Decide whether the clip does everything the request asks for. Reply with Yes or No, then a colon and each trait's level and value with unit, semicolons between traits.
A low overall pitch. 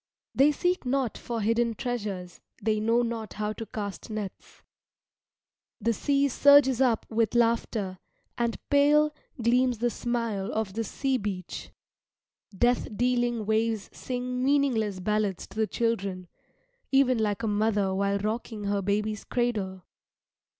No: high, 225 Hz